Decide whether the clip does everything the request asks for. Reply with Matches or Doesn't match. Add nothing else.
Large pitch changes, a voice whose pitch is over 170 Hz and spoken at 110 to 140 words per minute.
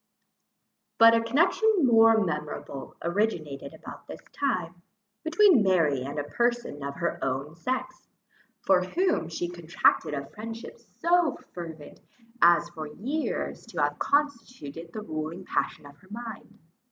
Matches